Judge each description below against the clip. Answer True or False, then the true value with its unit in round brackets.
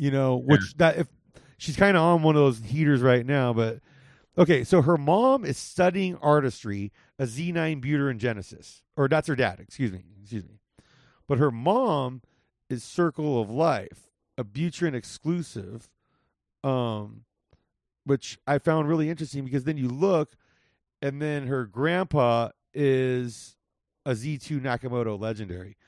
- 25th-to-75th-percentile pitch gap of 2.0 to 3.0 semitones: False (4.8 semitones)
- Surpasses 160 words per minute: False (155 wpm)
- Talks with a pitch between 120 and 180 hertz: True (140 Hz)